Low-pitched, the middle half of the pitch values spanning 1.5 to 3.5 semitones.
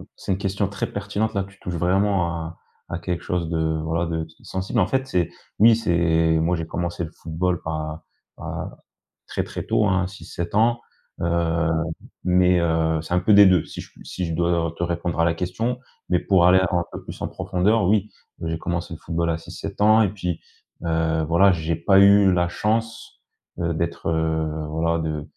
Yes: very low, 85 Hz; average, 2.9 semitones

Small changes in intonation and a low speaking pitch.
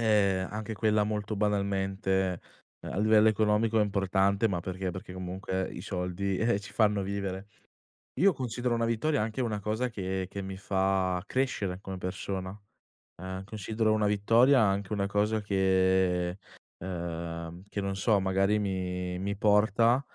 Yes: narrow, 2.3 semitones; low, 100 Hz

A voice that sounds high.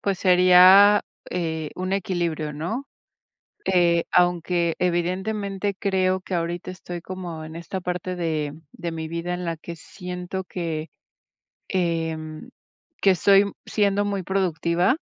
No: medium, 180 Hz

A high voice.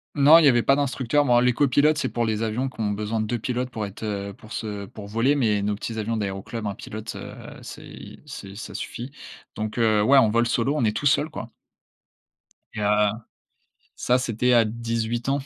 No: low, 115 Hz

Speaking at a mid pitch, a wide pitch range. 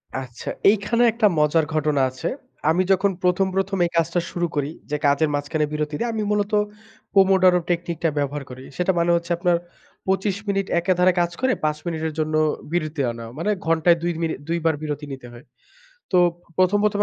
No: medium, 170 Hz; average, 3.9 semitones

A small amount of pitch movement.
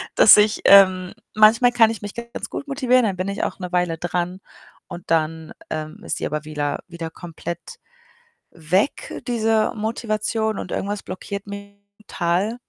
No: average, 4.1 semitones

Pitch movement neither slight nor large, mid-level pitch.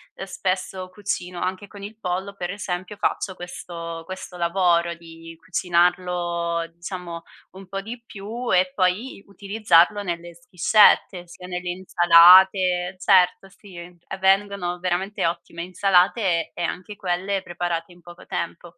No: narrow, 2.0 semitones; medium, 180 Hz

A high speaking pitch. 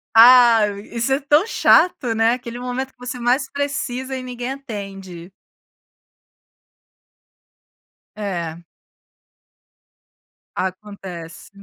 Yes: high, 240 Hz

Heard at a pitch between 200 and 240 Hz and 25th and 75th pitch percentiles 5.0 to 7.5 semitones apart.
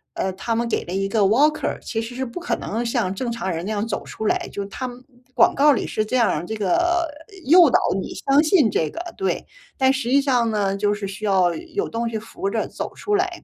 Yes: high, 230 Hz; wide, 5.4 semitones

